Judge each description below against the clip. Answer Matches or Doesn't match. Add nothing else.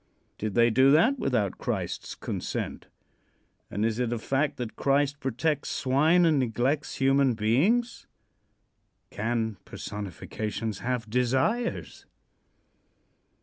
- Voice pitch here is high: Doesn't match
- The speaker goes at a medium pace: Doesn't match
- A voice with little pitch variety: Doesn't match